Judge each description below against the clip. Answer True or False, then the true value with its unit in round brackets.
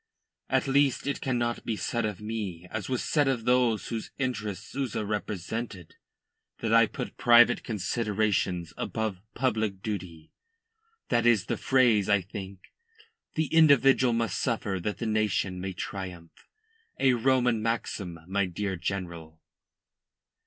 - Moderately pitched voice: False (110 Hz)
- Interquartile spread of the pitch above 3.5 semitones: True (4.0 semitones)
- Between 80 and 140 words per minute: True (135 wpm)